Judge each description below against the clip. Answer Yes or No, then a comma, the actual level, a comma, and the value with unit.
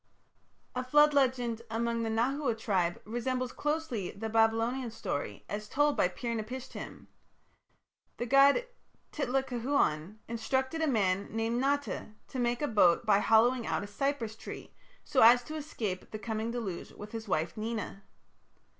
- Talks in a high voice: Yes, high, 235 Hz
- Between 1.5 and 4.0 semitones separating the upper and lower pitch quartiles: Yes, average, 3.4 semitones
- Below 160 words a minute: Yes, average, 145 wpm